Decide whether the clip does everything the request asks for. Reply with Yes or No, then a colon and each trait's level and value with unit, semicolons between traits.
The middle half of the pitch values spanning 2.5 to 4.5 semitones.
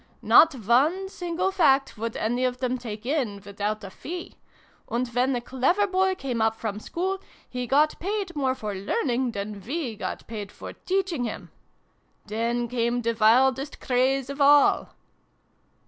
No: average, 5.1 semitones